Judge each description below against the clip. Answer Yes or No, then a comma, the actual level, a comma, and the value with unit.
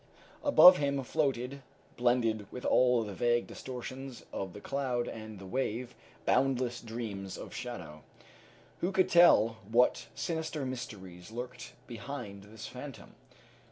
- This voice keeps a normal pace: No, slow, 125 wpm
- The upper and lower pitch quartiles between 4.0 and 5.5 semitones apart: No, average, 3.5 semitones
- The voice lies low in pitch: Yes, low, 120 Hz